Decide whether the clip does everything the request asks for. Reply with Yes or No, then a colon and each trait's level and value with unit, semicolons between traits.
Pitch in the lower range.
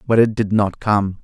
Yes: low, 105 Hz